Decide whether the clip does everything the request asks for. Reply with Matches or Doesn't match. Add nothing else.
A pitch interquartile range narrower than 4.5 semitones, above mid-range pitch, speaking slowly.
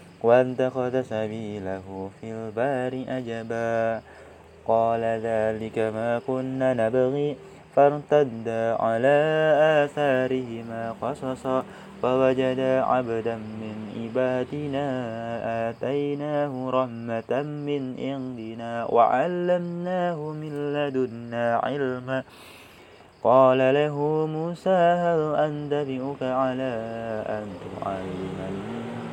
Doesn't match